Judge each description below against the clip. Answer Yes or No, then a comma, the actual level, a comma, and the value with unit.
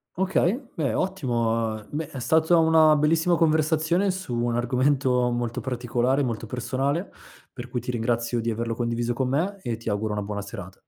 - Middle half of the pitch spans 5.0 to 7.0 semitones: Yes, average, 5.3 semitones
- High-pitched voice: No, low, 125 Hz